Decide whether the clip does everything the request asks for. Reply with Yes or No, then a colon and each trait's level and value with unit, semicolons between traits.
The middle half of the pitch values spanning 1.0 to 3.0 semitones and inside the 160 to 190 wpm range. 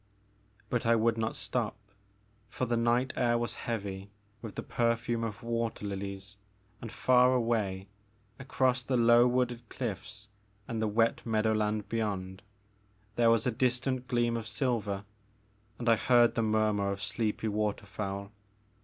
No: narrow, 2.4 semitones; average, 145 wpm